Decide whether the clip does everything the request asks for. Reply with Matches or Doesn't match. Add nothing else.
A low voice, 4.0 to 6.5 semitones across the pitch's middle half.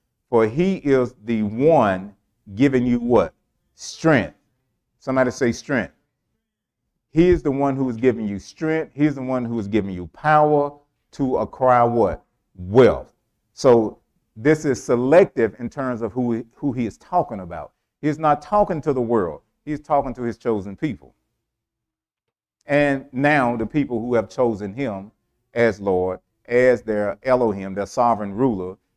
Matches